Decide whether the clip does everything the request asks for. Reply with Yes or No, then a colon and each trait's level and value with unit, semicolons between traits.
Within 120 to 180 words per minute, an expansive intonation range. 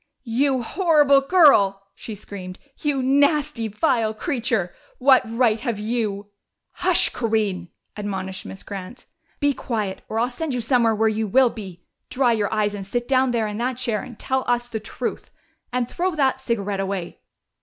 No: average, 170 wpm; average, 4.1 semitones